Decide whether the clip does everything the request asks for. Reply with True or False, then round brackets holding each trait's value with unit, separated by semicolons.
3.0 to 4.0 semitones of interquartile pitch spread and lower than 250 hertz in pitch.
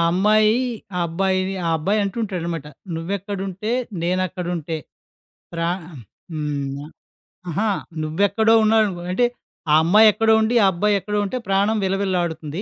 True (3.7 semitones; 190 Hz)